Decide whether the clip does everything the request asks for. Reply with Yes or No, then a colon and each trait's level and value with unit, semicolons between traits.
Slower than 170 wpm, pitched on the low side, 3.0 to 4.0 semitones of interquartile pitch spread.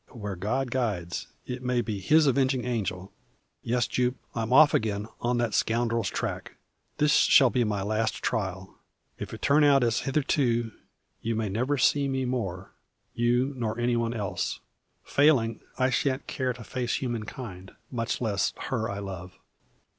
Yes: average, 160 wpm; low, 120 Hz; average, 3.4 semitones